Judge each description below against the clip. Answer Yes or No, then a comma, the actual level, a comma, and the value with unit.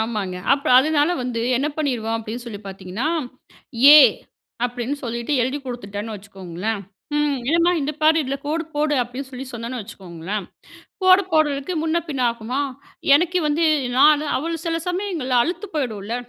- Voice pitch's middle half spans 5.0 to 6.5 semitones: Yes, wide, 5.4 semitones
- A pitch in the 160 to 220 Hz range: No, very high, 260 Hz